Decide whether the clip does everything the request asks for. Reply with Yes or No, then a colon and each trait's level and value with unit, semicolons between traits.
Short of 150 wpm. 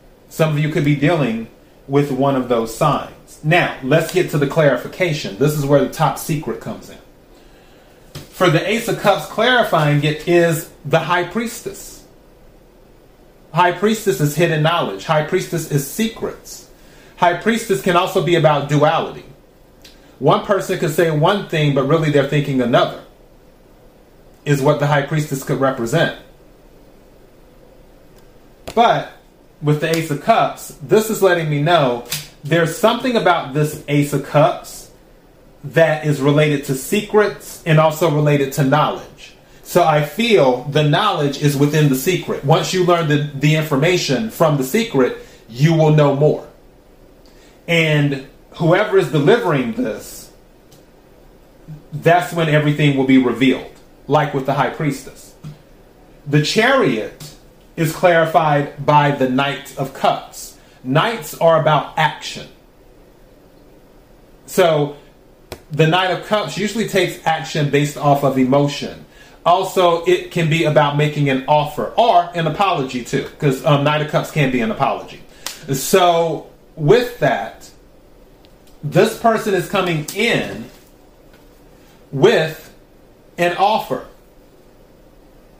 Yes: slow, 135 wpm